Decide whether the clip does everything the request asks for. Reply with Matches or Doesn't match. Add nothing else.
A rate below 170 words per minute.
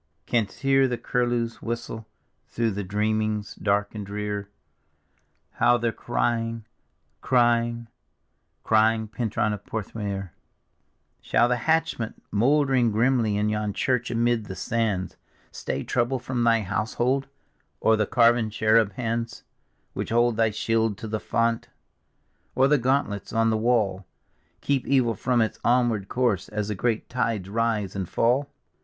Matches